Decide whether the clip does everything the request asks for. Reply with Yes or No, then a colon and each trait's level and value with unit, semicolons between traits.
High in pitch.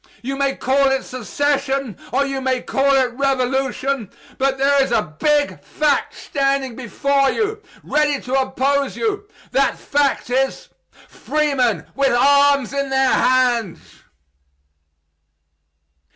Yes: very high, 270 Hz